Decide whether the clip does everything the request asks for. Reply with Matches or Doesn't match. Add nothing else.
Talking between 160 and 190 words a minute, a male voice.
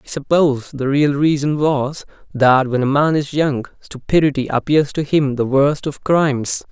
Matches